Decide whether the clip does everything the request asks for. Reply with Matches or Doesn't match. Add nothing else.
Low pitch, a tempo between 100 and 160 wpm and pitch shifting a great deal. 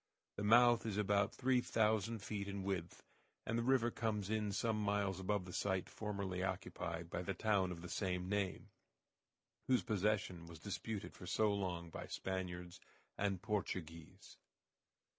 Doesn't match